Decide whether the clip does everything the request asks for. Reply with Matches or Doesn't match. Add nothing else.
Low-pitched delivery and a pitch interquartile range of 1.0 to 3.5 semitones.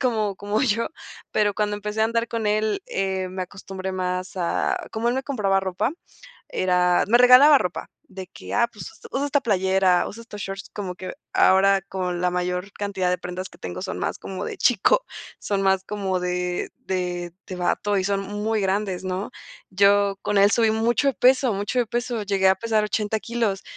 Doesn't match